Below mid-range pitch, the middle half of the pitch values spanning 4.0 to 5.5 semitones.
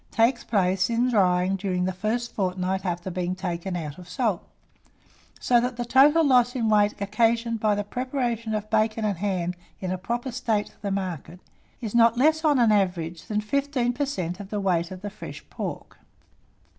No: high, 210 Hz; average, 4.5 semitones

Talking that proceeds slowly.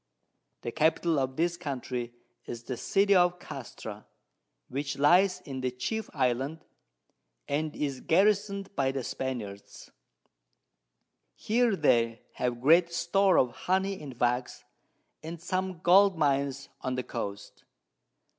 Yes: slow, 125 wpm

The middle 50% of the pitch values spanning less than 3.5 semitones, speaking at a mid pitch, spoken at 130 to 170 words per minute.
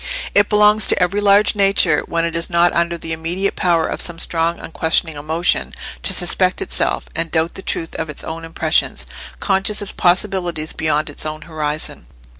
No: average, 3.0 semitones; medium, 170 Hz; average, 180 wpm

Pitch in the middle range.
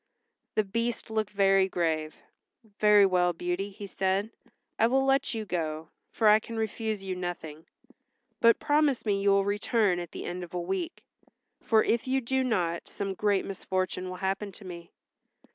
No: high, 195 Hz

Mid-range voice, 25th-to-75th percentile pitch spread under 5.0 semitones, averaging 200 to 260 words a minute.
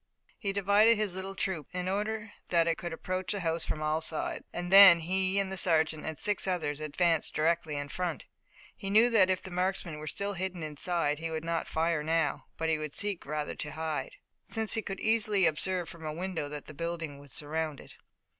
Yes: medium, 170 Hz; average, 3.4 semitones; fast, 205 wpm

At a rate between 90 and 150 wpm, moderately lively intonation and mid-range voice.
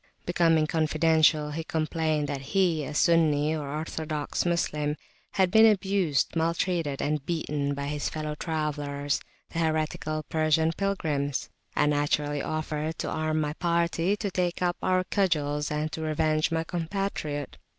No: average, 140 wpm; narrow, 2.2 semitones; medium, 155 Hz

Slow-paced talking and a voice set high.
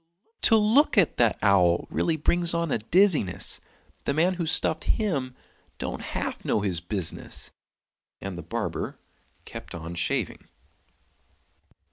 No: slow, 130 wpm; medium, 140 Hz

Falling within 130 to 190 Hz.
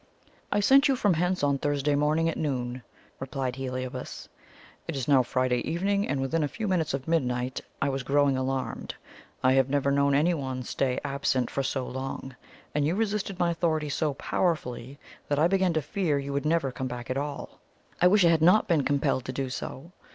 Yes: medium, 140 Hz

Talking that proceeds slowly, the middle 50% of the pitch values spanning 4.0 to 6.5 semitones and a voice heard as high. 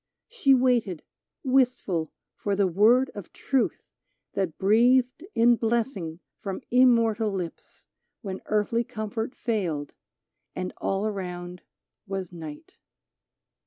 Yes: slow, 105 wpm; average, 4.7 semitones; high, 210 Hz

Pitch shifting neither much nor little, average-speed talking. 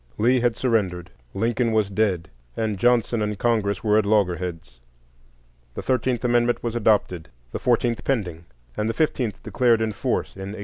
Yes: average, 3.3 semitones; average, 165 wpm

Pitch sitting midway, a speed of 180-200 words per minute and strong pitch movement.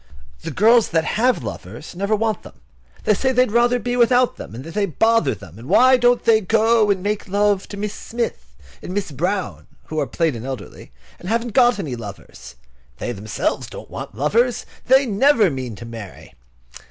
No: high, 205 Hz; average, 190 wpm; wide, 8.8 semitones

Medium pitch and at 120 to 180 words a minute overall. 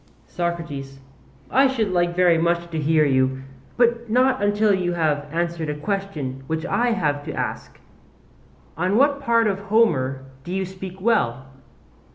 Yes: medium, 175 Hz; average, 155 wpm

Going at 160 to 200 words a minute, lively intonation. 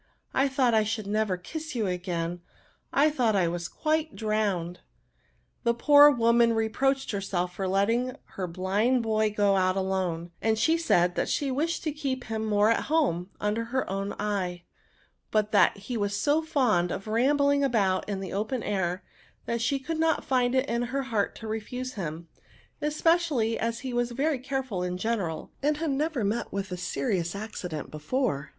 Yes: average, 175 wpm; wide, 5.7 semitones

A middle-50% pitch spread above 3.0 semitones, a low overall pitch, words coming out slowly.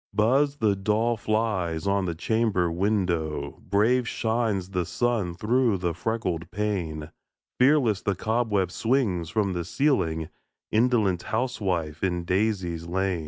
Yes: average, 4.4 semitones; low, 100 Hz; slow, 125 wpm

